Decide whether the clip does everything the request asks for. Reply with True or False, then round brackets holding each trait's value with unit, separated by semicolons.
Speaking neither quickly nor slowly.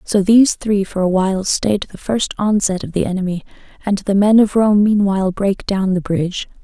False (210 wpm)